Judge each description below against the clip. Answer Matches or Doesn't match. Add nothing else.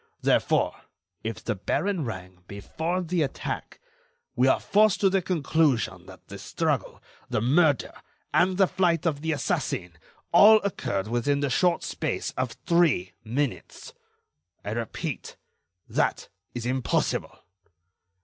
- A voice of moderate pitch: Matches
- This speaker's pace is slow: Matches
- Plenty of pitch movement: Matches